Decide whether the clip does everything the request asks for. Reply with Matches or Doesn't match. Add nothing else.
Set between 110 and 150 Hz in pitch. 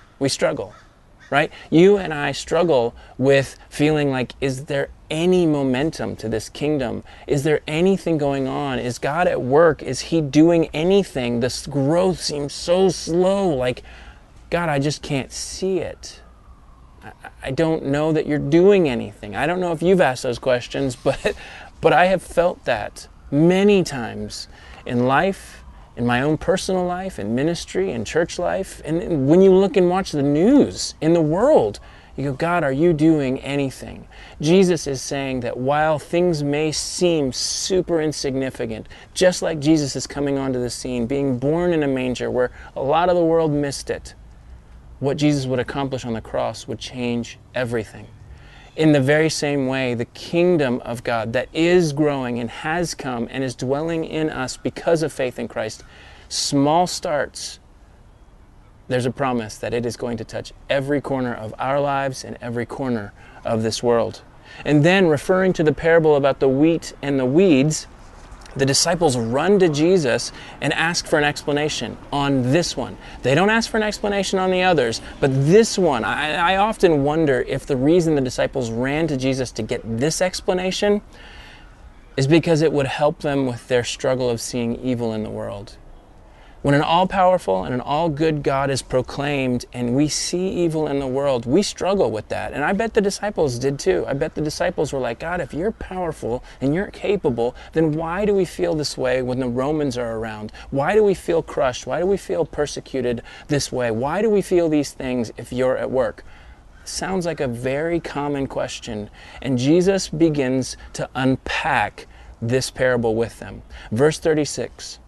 Matches